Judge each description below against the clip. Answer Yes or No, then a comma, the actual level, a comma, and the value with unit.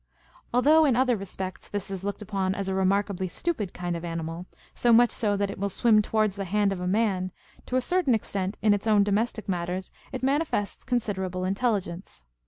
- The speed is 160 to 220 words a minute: Yes, average, 195 wpm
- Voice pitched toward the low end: No, high, 200 Hz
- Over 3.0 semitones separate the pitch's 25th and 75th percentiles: Yes, average, 3.4 semitones